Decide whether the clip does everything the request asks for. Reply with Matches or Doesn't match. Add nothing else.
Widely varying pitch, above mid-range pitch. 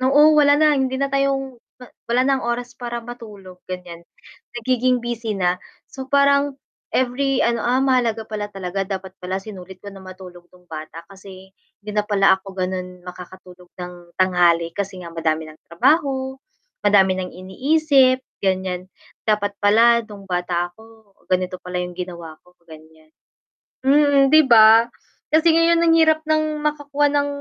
Matches